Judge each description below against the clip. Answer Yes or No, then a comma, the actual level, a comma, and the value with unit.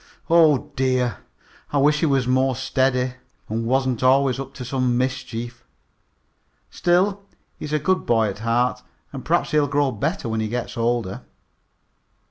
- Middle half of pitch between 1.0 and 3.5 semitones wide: Yes, average, 2.9 semitones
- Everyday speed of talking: Yes, average, 150 wpm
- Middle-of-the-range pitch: No, low, 130 Hz